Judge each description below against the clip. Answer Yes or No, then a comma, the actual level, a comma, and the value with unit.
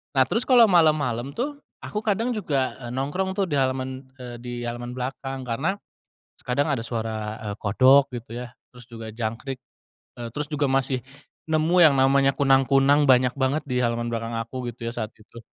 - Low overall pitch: Yes, low, 130 Hz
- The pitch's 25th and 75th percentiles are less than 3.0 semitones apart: No, average, 3.3 semitones